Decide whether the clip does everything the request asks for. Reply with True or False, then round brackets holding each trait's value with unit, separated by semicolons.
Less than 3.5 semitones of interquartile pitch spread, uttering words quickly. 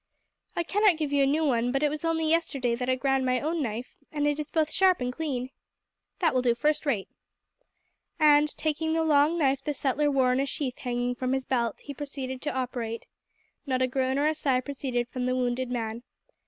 True (3.1 semitones; 220 wpm)